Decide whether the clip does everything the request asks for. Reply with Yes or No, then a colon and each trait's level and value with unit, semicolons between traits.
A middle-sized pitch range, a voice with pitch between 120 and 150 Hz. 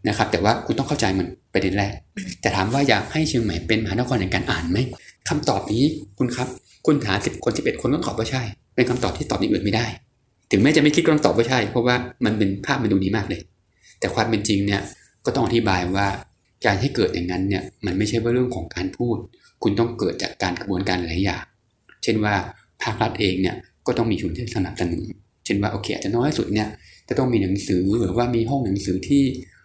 No: average, 4.2 semitones; low, 110 Hz